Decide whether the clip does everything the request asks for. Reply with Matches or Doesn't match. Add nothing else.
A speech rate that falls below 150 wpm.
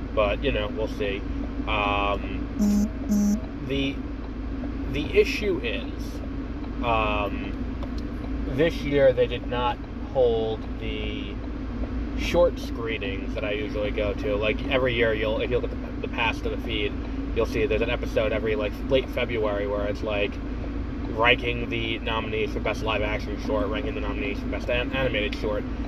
Doesn't match